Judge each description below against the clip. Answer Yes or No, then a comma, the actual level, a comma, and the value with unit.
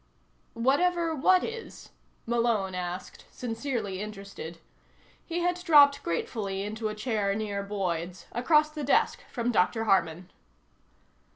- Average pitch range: No, wide, 6.5 semitones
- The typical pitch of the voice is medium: No, high, 225 Hz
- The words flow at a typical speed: No, slow, 115 wpm